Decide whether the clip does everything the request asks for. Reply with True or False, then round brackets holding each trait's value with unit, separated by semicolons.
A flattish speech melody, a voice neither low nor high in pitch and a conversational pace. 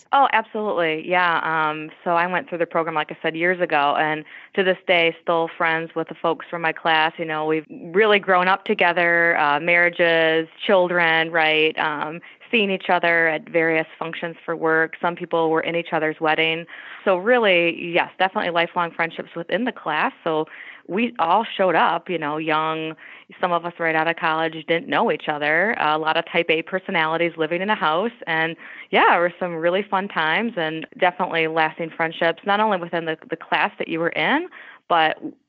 True (2.0 semitones; 170 Hz; 195 wpm)